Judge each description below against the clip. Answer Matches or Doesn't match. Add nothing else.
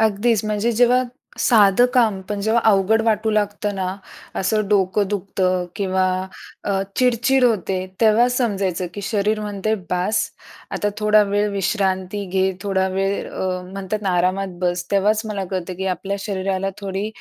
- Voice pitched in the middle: Doesn't match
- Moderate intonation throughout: Doesn't match